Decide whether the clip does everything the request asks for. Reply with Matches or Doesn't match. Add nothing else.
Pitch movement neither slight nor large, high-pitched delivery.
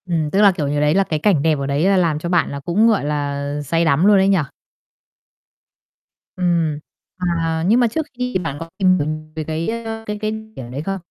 Doesn't match